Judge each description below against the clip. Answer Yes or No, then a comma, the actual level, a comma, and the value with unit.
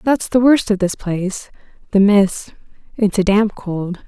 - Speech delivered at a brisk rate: No, average, 145 wpm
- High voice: Yes, high, 205 Hz